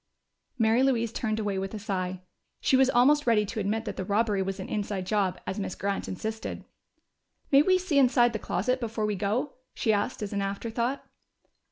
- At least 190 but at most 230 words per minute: Yes, average, 195 wpm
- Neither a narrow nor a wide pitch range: Yes, average, 3.5 semitones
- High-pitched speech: Yes, high, 215 Hz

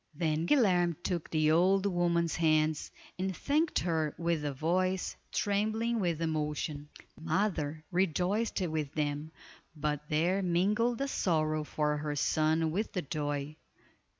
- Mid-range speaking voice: Yes, medium, 165 Hz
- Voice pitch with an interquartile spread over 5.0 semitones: No, average, 3.5 semitones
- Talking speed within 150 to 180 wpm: No, slow, 135 wpm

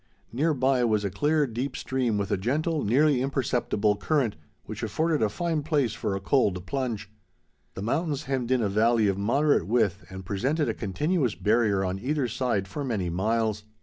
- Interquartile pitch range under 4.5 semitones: No, wide, 5.5 semitones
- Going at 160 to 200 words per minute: Yes, average, 180 wpm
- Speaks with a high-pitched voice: No, low, 120 Hz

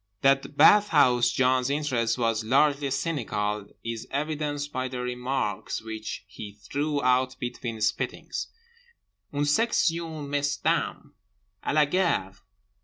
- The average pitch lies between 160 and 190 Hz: No, low, 135 Hz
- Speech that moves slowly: Yes, slow, 110 wpm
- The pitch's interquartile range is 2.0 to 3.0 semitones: No, average, 3.6 semitones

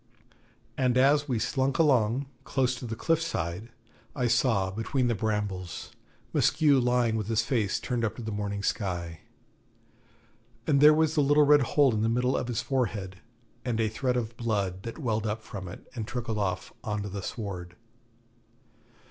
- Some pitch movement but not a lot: Yes, average, 4.2 semitones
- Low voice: Yes, low, 115 Hz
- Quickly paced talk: No, average, 175 wpm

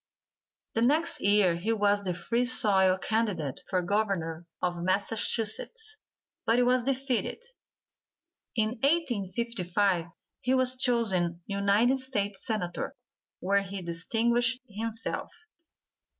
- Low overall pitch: No, high, 210 Hz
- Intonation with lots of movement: No, average, 4.6 semitones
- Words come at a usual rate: No, slow, 105 wpm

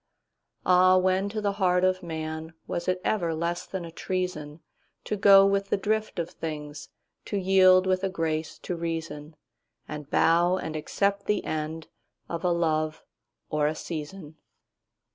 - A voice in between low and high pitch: Yes, medium, 170 Hz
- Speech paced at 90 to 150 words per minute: Yes, average, 140 wpm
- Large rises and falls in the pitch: No, average, 3.0 semitones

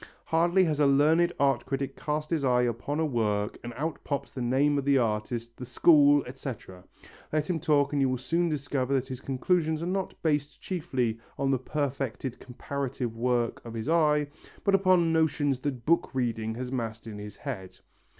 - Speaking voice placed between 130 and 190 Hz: Yes, medium, 140 Hz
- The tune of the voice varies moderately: Yes, average, 3.9 semitones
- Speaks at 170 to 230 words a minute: Yes, average, 190 wpm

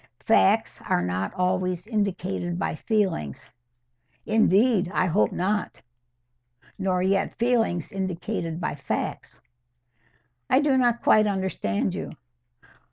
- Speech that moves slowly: Yes, slow, 105 wpm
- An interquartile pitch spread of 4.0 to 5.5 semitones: No, average, 3.5 semitones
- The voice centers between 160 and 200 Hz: Yes, high, 190 Hz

